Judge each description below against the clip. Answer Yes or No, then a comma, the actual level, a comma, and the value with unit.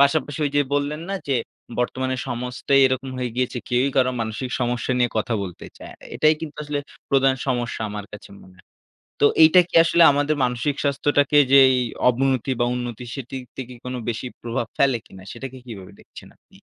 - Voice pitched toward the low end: Yes, low, 130 Hz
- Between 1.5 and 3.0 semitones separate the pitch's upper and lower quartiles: Yes, narrow, 2.6 semitones